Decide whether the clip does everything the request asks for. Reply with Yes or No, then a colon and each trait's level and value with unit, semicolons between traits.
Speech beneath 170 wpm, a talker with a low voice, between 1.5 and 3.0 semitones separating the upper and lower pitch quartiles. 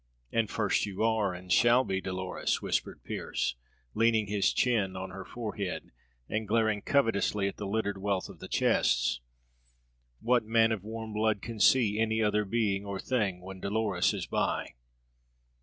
Yes: average, 160 wpm; low, 105 Hz; narrow, 2.5 semitones